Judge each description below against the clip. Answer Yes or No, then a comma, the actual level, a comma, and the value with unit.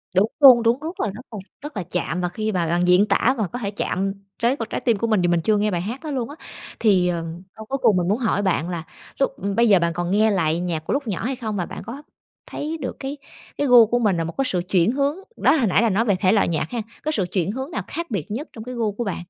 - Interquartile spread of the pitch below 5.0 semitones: No, average, 5.3 semitones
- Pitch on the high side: Yes, high, 215 Hz